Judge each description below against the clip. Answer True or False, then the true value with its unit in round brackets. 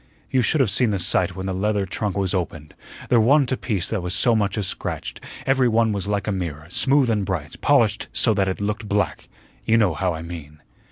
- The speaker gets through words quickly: True (230 wpm)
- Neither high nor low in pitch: False (100 Hz)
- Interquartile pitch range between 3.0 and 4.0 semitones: True (3.7 semitones)